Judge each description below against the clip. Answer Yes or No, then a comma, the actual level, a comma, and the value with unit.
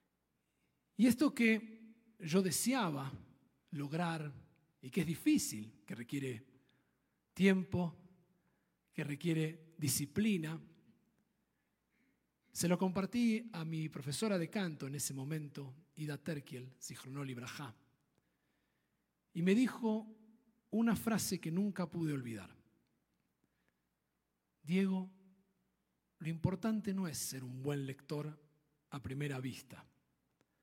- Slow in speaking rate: Yes, slow, 100 wpm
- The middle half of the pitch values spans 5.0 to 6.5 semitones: Yes, wide, 5.6 semitones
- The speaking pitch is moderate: Yes, medium, 160 Hz